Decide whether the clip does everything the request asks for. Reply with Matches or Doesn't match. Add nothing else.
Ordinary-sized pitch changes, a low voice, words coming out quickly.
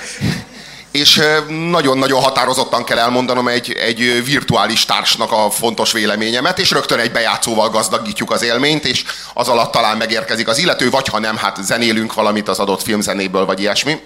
Matches